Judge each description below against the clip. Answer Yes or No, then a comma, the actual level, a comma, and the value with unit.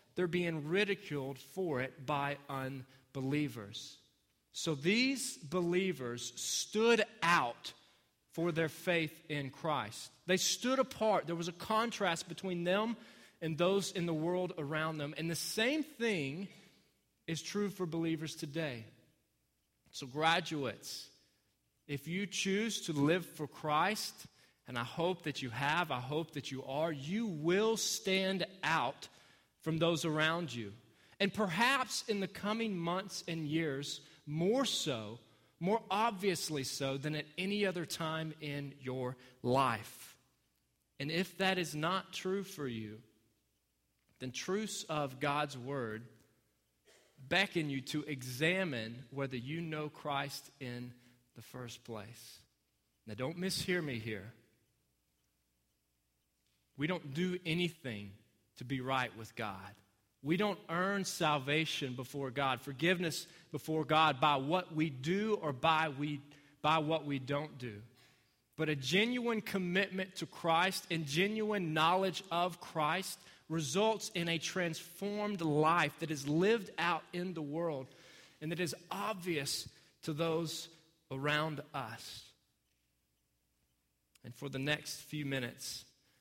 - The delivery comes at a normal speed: No, slow, 130 wpm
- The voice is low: No, medium, 155 Hz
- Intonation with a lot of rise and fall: Yes, wide, 5.8 semitones